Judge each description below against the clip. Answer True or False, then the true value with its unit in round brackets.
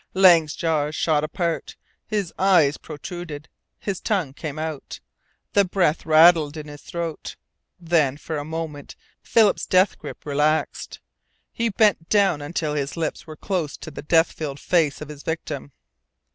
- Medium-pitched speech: True (160 Hz)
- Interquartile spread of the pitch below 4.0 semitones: True (2.9 semitones)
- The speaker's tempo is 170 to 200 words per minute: False (150 wpm)